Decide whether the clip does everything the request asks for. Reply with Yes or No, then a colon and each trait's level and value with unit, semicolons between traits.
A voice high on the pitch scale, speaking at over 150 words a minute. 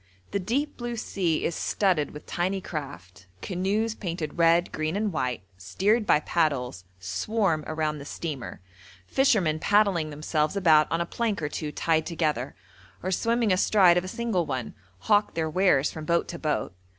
No: medium, 170 Hz; average, 165 wpm